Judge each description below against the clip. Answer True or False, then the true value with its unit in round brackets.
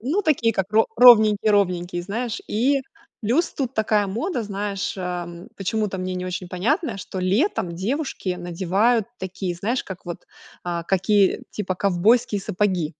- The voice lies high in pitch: True (200 Hz)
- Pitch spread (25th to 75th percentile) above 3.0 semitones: True (3.8 semitones)